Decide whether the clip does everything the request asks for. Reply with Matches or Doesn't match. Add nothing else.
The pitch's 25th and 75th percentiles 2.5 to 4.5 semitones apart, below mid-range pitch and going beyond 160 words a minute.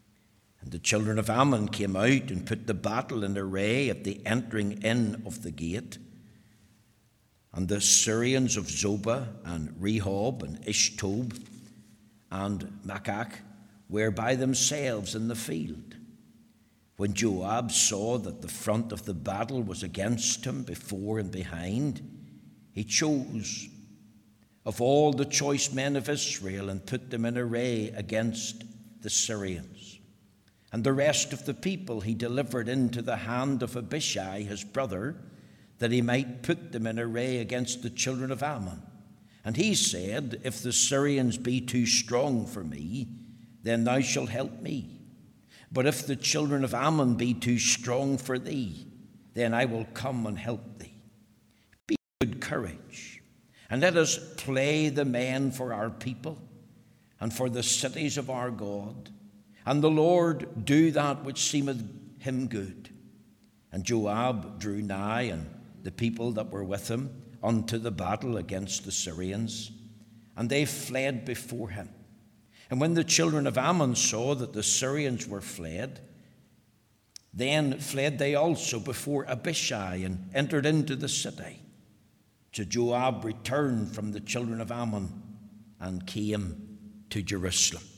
Doesn't match